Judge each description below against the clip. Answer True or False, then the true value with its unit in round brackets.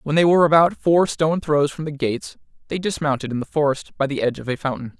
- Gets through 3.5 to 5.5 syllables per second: False (6.6 syllables/s)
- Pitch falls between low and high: True (150 Hz)